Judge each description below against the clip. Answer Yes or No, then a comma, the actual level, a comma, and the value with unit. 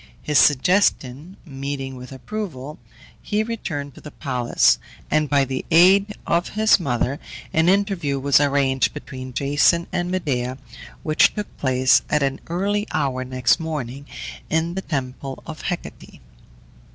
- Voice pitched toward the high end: No, medium, 145 Hz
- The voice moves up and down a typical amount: Yes, average, 4.8 semitones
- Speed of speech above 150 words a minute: No, average, 140 wpm